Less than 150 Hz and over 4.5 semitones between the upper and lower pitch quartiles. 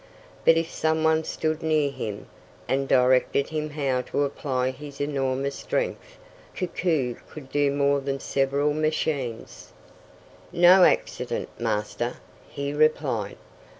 No: medium, 140 Hz; average, 2.9 semitones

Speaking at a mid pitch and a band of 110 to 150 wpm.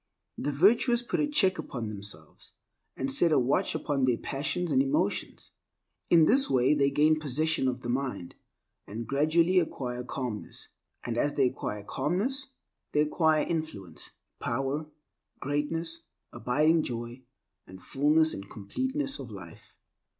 Yes: medium, 145 Hz; average, 140 wpm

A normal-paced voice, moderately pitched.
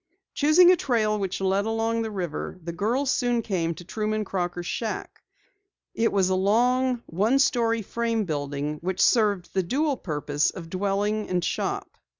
No: average, 160 wpm; high, 210 Hz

